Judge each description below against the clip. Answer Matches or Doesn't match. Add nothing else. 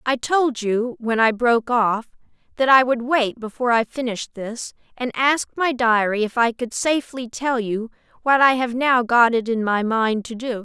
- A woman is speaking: Matches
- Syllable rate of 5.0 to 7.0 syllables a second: Doesn't match